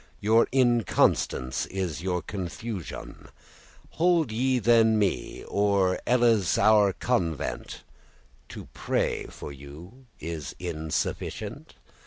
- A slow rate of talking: Yes, slow, 90 wpm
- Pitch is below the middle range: Yes, low, 100 Hz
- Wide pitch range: Yes, wide, 5.8 semitones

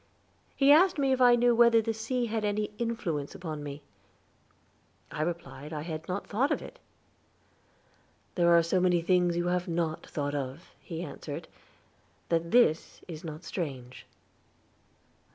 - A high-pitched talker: No, medium, 175 Hz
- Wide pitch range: Yes, wide, 6.4 semitones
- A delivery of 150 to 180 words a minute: Yes, average, 155 wpm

